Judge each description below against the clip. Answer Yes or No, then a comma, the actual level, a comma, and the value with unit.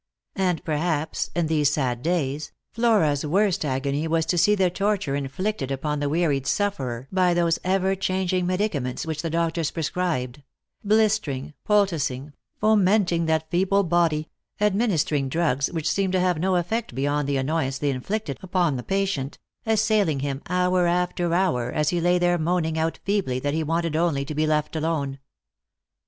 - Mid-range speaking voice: Yes, medium, 165 Hz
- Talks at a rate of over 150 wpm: Yes, average, 165 wpm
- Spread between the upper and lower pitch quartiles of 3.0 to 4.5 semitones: Yes, average, 4.2 semitones